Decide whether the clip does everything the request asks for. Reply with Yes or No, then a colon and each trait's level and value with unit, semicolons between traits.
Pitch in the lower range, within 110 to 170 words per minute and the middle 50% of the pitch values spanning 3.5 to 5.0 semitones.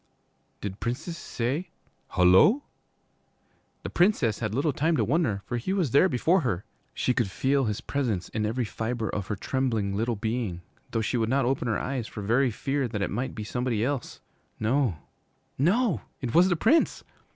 No: low, 120 Hz; average, 180 wpm; average, 4.6 semitones